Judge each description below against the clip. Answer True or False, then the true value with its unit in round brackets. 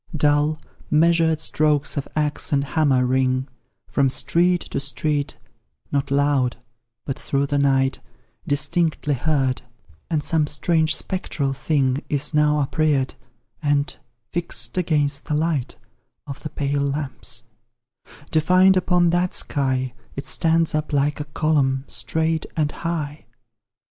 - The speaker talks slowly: True (125 wpm)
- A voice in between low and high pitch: True (150 Hz)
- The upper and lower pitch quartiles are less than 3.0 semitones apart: True (2.4 semitones)